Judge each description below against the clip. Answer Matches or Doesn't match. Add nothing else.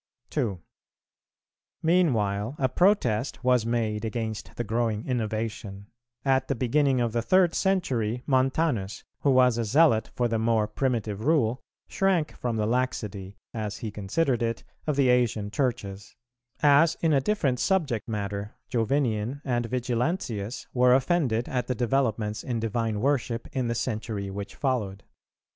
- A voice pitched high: Doesn't match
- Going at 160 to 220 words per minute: Doesn't match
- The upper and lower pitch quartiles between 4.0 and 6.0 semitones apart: Doesn't match